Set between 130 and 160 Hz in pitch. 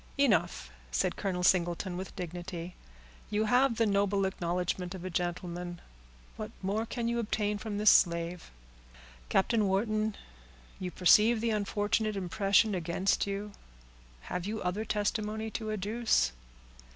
No: high, 195 Hz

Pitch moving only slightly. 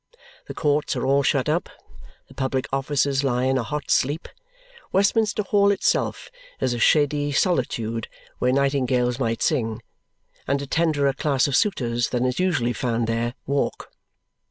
No: average, 3.3 semitones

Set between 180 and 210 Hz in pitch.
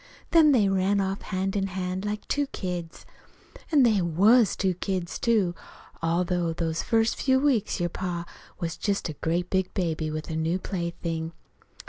Yes: medium, 185 Hz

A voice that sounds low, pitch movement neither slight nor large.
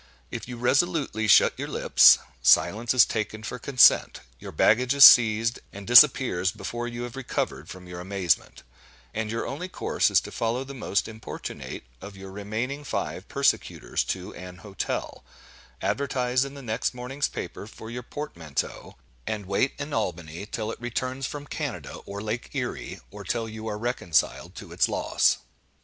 Yes: low, 115 Hz; average, 4.1 semitones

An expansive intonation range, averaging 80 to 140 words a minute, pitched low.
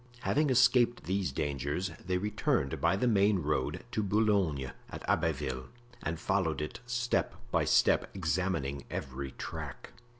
Yes: wide, 6.8 semitones; slow, 135 wpm; very low, 90 Hz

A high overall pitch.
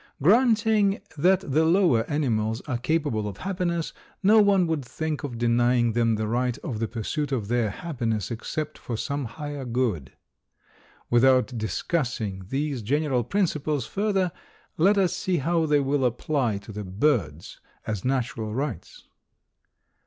No: low, 135 Hz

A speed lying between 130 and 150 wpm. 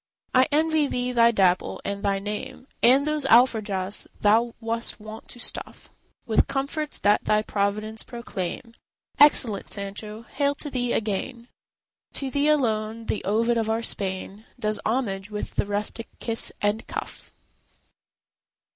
Yes: average, 140 wpm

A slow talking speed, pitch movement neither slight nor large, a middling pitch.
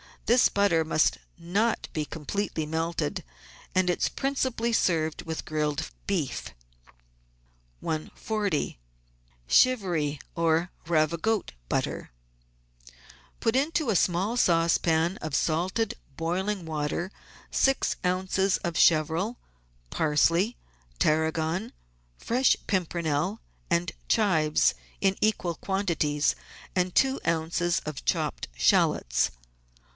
Yes: slow, 100 wpm; average, 4.1 semitones; medium, 170 Hz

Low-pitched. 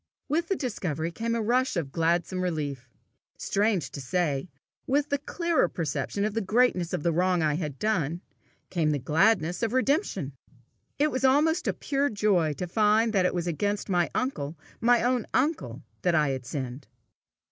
No: medium, 185 Hz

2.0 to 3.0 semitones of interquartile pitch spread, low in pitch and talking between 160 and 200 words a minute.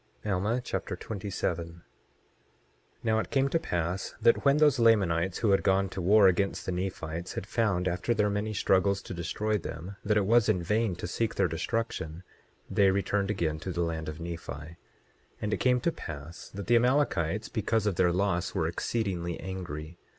No: average, 4.0 semitones; very low, 95 Hz; average, 185 wpm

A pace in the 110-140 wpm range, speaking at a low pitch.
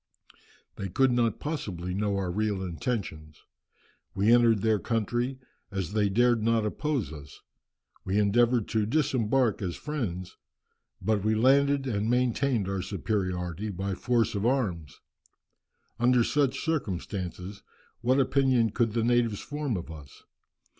Yes: slow, 135 wpm; low, 110 Hz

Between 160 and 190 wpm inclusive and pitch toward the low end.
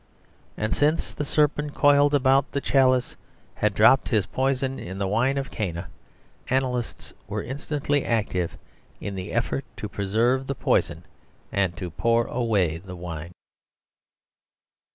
No: slow, 135 wpm; low, 120 Hz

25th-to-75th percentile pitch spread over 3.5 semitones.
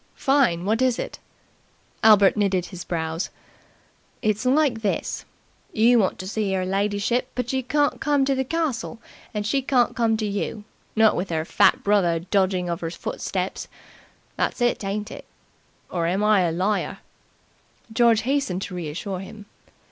Yes: average, 4.5 semitones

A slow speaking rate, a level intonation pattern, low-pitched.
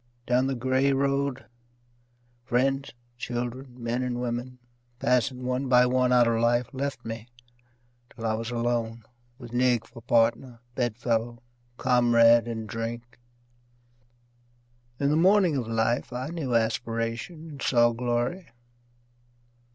Yes: slow, 130 wpm; narrow, 1.8 semitones; low, 120 Hz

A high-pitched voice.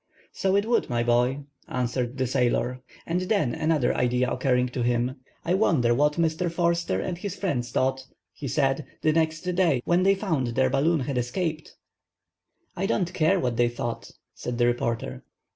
No: low, 135 Hz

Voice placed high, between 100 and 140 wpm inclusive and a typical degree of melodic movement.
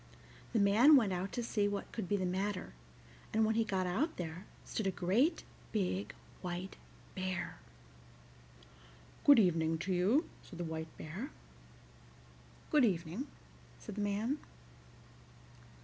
Yes: high, 195 Hz; slow, 135 wpm; average, 3.6 semitones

